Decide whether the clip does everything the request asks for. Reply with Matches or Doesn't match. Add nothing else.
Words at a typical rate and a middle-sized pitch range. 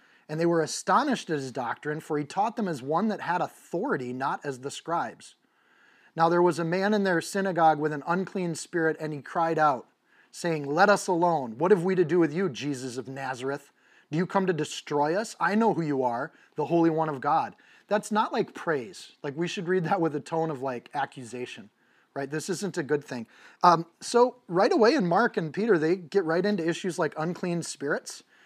Doesn't match